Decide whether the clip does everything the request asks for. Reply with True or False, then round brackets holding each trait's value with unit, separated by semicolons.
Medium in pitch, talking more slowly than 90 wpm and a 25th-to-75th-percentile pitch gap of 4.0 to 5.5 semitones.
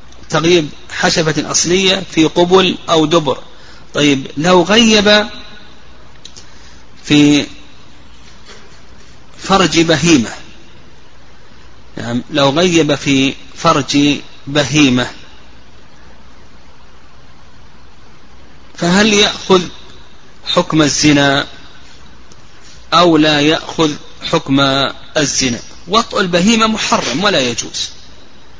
True (155 Hz; 70 wpm; 4.5 semitones)